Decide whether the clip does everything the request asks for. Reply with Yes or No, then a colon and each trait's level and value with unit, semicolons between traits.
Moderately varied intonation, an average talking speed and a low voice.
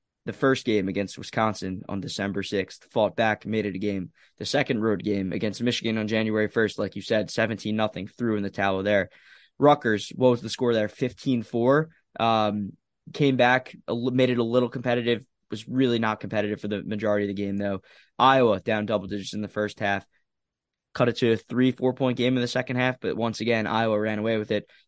No: average, 3.0 semitones; fast, 210 wpm; low, 110 Hz